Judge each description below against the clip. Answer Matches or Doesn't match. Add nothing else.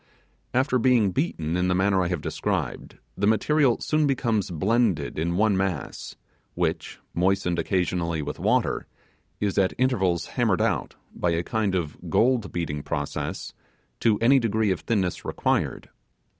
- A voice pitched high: Doesn't match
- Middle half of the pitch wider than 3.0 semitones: Matches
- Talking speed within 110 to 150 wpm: Matches